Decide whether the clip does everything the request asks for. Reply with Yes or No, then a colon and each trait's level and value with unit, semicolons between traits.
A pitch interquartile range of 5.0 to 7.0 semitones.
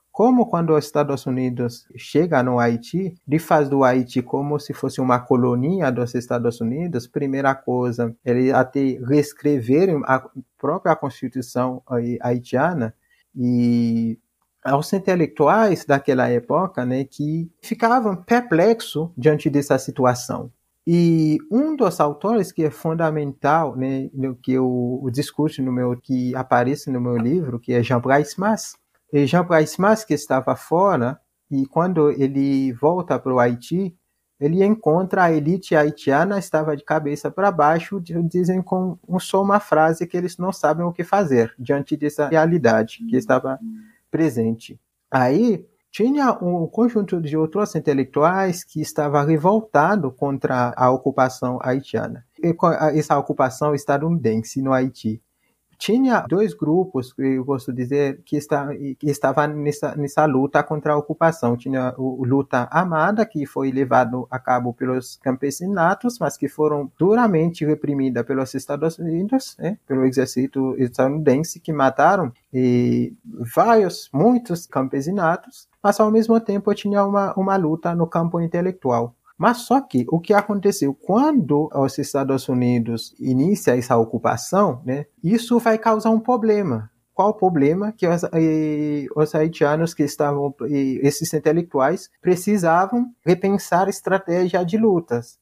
Yes: wide, 5.4 semitones